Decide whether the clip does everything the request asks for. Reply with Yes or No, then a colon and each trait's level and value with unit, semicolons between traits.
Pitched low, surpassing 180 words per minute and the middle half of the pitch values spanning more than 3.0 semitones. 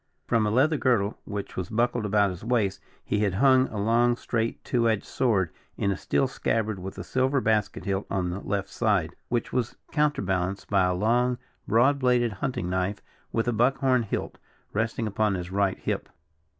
Yes: low, 110 Hz; average, 190 wpm; average, 3.7 semitones